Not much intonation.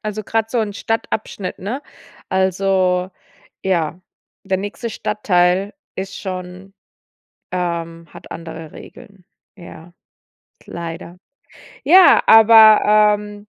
No: average, 3.0 semitones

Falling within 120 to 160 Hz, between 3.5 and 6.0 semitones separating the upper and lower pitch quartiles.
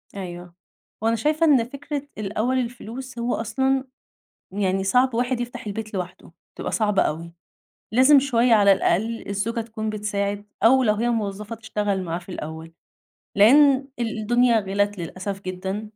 No: high, 220 Hz; average, 3.8 semitones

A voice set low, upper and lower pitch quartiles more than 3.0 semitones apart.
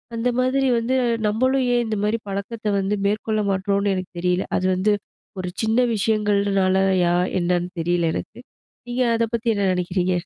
No: high, 200 Hz; average, 3.4 semitones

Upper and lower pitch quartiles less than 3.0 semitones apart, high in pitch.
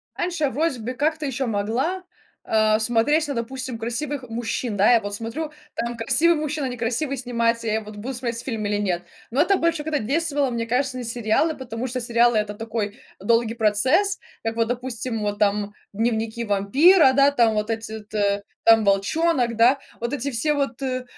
No: average, 4.0 semitones; high, 235 Hz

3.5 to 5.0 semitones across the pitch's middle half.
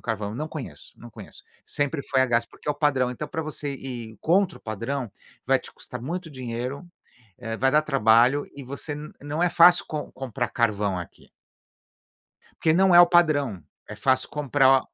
Yes: average, 4.4 semitones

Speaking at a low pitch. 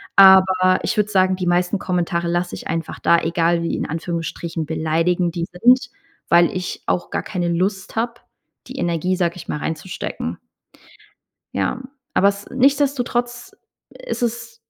No: medium, 180 Hz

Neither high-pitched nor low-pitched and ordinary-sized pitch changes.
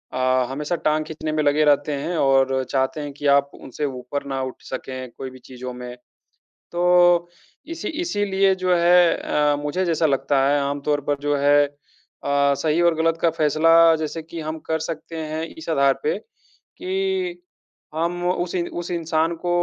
Yes: medium, 155 Hz; average, 3.3 semitones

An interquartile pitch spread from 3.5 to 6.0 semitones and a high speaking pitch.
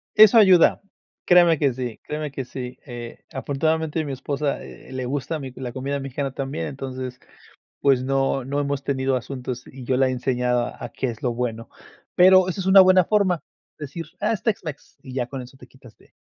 No: average, 3.8 semitones; low, 135 Hz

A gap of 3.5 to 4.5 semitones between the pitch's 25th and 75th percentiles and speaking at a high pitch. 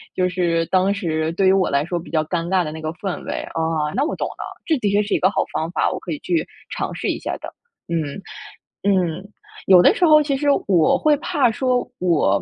No: average, 3.8 semitones; medium, 180 Hz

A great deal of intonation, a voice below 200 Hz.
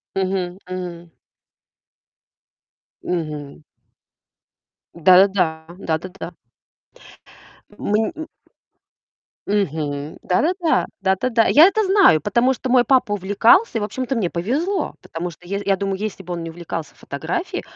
Yes: wide, 5.8 semitones; high, 190 Hz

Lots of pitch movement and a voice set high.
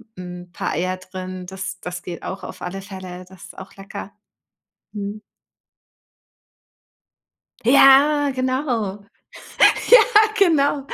Yes: wide, 6.0 semitones; high, 195 Hz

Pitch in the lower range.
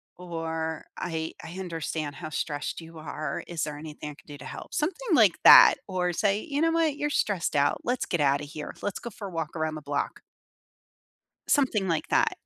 No: medium, 165 Hz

